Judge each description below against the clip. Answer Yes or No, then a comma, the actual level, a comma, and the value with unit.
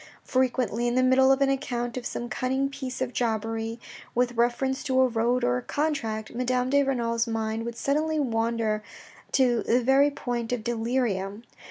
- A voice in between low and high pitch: No, high, 245 Hz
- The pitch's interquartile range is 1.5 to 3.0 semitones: Yes, narrow, 2.5 semitones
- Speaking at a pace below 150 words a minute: No, average, 175 wpm